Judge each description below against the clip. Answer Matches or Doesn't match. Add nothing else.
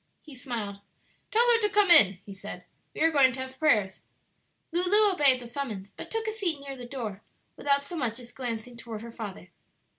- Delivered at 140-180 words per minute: Doesn't match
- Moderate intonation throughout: Doesn't match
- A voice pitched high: Matches